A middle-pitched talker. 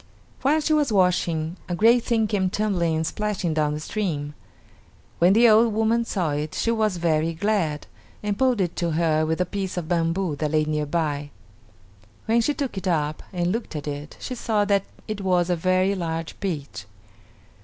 Yes: medium, 180 Hz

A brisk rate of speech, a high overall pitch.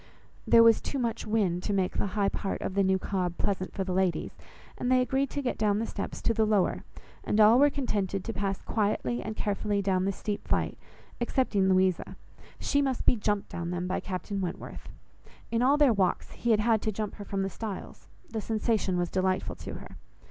Yes: fast, 215 wpm; high, 205 Hz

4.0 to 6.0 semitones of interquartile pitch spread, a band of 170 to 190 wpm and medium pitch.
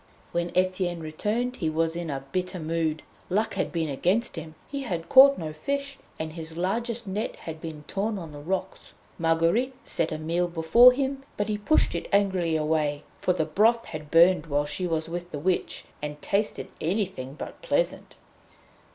Yes: average, 4.7 semitones; average, 180 wpm; medium, 175 Hz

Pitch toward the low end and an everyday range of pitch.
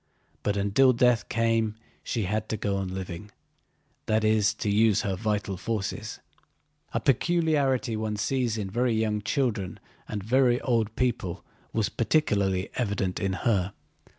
Yes: low, 110 Hz; average, 3.0 semitones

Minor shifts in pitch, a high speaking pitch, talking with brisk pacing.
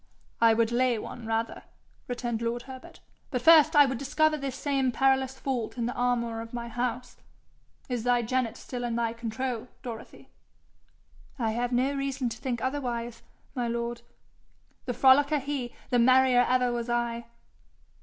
No: narrow, 2.0 semitones; high, 245 Hz; average, 160 wpm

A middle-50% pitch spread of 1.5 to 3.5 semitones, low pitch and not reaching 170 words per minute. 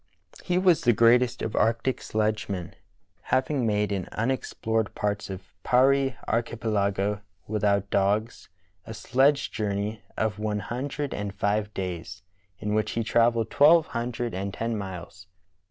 Yes: average, 2.9 semitones; low, 110 Hz; slow, 135 wpm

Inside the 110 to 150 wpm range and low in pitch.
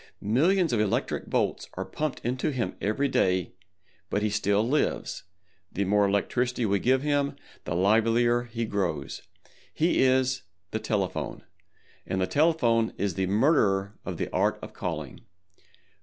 Yes: average, 140 wpm; low, 110 Hz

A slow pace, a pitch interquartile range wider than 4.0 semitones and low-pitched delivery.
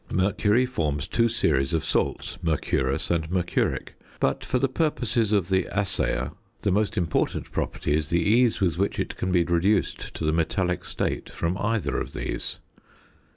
No: average, 165 wpm; average, 4.7 semitones; very low, 90 Hz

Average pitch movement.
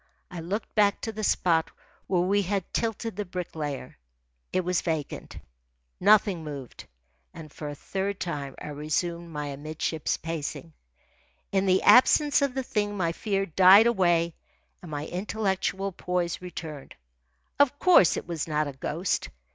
Yes: average, 4.2 semitones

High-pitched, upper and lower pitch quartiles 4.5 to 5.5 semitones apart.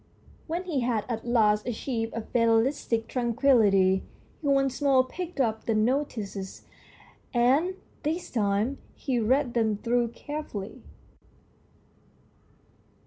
No: high, 240 Hz; average, 3.8 semitones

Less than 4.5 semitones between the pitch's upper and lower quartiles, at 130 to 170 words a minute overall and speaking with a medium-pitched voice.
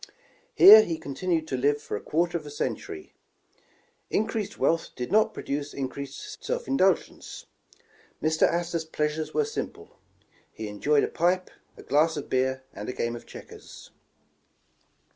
No: average, 4.8 semitones; average, 150 wpm; medium, 155 Hz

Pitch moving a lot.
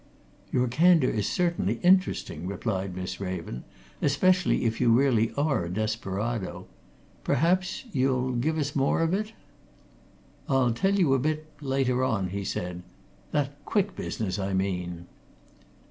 Yes: wide, 7.8 semitones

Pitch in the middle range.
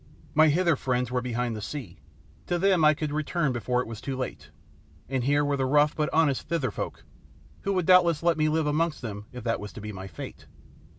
Yes: medium, 145 Hz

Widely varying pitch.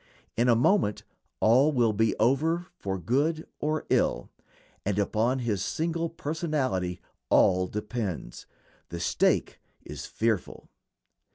Yes: wide, 7.1 semitones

